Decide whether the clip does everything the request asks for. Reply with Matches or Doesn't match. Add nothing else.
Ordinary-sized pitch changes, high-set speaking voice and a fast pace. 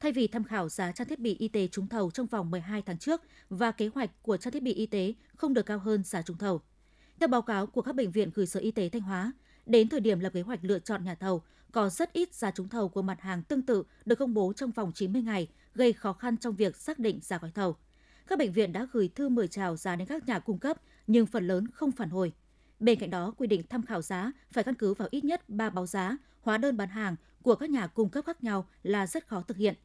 Matches